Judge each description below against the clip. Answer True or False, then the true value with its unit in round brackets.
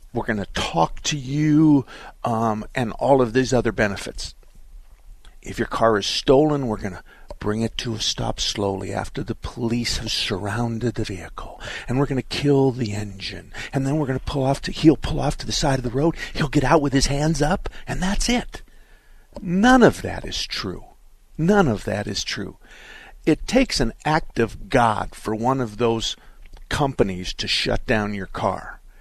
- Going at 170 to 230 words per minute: True (190 wpm)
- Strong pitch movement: True (5.7 semitones)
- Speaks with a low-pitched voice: True (120 Hz)